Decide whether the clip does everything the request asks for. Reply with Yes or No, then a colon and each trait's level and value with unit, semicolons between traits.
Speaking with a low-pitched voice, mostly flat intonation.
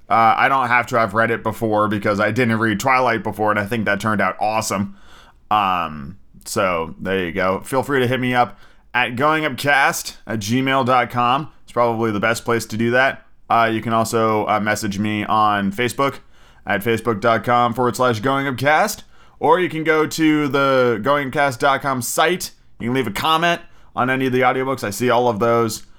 No: low, 120 Hz; average, 3.6 semitones